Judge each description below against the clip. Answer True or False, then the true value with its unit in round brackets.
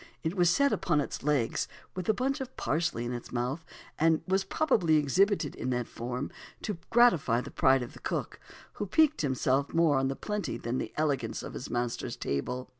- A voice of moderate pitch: True (150 Hz)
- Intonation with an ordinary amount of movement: False (7.2 semitones)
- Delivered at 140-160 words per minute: False (195 wpm)